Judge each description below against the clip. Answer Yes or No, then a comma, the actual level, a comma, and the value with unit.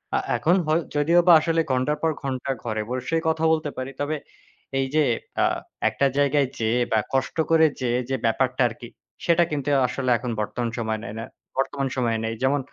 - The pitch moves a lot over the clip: No, average, 3.8 semitones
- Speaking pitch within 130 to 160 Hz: Yes, low, 135 Hz